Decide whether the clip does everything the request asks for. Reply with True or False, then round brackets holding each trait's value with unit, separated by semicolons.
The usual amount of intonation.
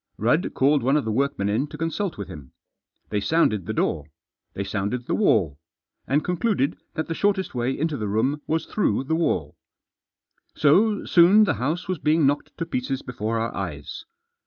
False (7.2 semitones)